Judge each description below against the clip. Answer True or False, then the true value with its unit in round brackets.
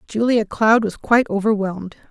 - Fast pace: False (140 wpm)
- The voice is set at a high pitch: True (215 Hz)